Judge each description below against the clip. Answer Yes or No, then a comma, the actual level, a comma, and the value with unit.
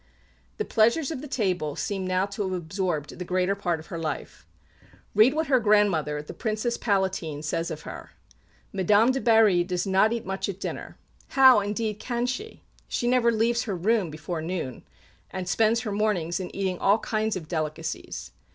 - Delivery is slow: No, average, 180 wpm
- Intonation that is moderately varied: Yes, average, 4.4 semitones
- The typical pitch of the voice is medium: No, high, 200 Hz